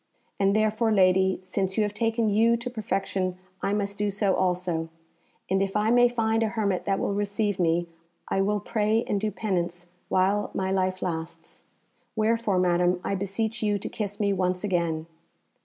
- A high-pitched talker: Yes, high, 200 Hz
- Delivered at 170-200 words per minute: Yes, average, 175 wpm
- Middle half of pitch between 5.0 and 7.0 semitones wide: No, narrow, 2.6 semitones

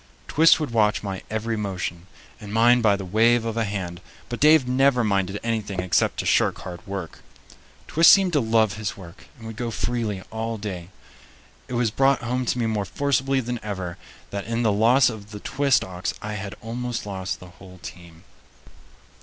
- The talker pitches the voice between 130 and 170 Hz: No, low, 110 Hz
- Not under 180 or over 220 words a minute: Yes, average, 190 wpm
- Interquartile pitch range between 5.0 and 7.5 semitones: No, average, 3.7 semitones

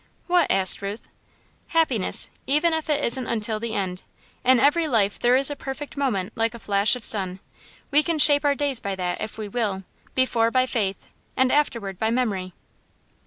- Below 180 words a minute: No, average, 185 wpm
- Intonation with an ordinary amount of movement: No, wide, 5.9 semitones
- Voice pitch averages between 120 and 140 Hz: No, high, 235 Hz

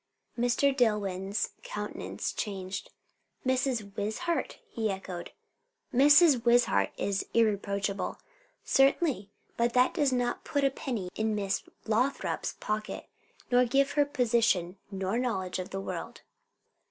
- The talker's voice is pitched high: Yes, high, 230 Hz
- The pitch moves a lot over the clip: No, average, 4.7 semitones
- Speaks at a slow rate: Yes, slow, 115 wpm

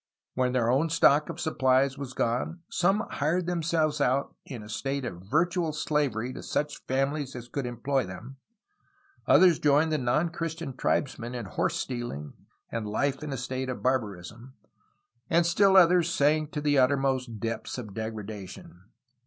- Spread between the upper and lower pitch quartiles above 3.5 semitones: Yes, average, 4.3 semitones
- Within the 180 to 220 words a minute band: No, average, 160 wpm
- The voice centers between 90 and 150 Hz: Yes, low, 135 Hz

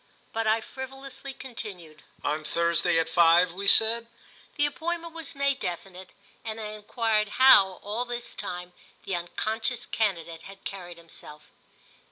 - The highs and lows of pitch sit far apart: Yes, wide, 5.8 semitones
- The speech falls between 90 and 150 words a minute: Yes, average, 140 wpm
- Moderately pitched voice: No, high, 210 Hz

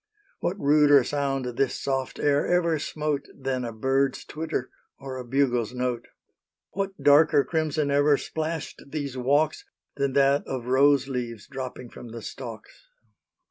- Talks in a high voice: No, medium, 140 Hz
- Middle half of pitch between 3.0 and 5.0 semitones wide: No, narrow, 2.6 semitones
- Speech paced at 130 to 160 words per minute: Yes, average, 140 wpm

